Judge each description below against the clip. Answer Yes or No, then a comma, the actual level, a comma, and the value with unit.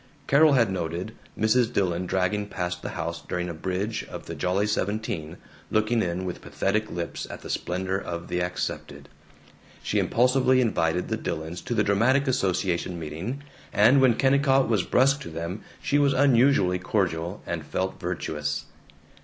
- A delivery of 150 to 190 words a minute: Yes, average, 160 wpm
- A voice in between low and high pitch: No, very low, 95 Hz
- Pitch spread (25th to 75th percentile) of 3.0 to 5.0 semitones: No, wide, 5.4 semitones